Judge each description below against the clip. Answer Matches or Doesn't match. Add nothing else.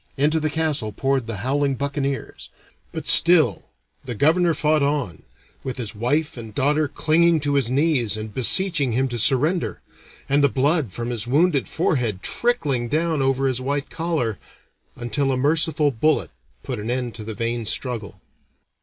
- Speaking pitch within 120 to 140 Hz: Matches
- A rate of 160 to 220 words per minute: Matches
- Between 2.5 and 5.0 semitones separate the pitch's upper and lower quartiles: Matches